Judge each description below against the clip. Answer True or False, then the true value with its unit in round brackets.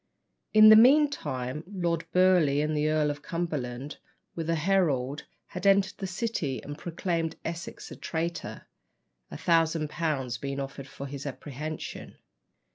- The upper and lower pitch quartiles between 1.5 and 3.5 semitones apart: False (3.9 semitones)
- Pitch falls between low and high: True (160 Hz)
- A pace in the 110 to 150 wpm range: True (140 wpm)